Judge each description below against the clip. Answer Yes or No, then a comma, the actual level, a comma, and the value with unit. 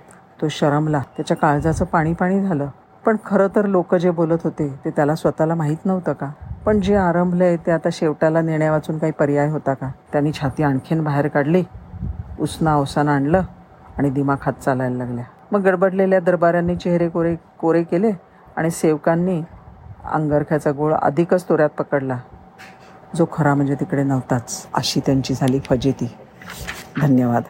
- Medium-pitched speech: Yes, medium, 155 Hz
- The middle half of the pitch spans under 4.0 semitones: Yes, average, 3.4 semitones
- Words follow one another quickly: Yes, fast, 150 wpm